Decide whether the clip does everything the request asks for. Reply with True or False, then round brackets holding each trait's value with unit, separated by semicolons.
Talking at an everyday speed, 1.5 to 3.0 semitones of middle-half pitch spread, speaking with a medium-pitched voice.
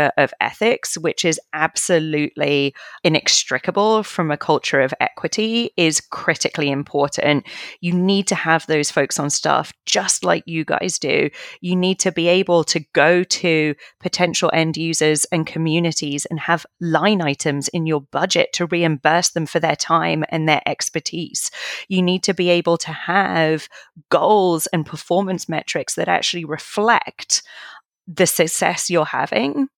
True (150 wpm; 2.7 semitones; 165 Hz)